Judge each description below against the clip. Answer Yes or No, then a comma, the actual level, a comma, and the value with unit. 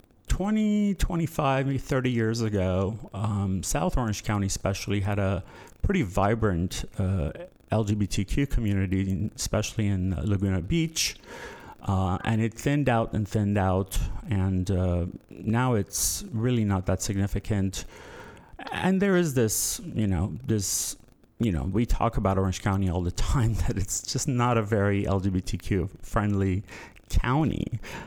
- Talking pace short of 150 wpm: Yes, slow, 135 wpm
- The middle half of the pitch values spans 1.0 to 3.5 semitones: Yes, average, 3.2 semitones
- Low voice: Yes, low, 105 Hz